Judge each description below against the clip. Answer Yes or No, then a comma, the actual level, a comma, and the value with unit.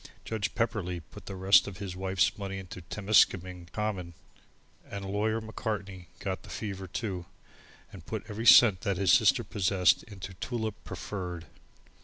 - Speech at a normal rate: Yes, average, 150 wpm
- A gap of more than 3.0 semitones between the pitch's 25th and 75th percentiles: No, narrow, 2.6 semitones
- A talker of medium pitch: No, very low, 95 Hz